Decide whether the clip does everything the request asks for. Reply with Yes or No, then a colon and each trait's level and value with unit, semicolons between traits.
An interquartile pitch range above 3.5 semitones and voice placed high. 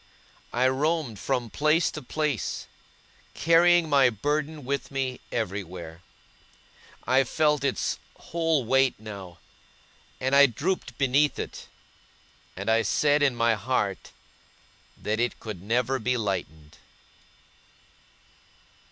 No: average, 5.0 semitones; low, 130 Hz